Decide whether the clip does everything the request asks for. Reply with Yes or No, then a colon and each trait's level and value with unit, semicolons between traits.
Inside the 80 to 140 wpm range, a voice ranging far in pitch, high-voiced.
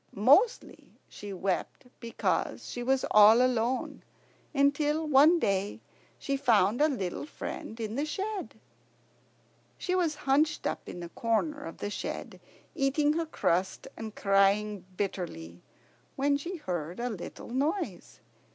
Yes: slow, 135 wpm; wide, 6.9 semitones; high, 245 Hz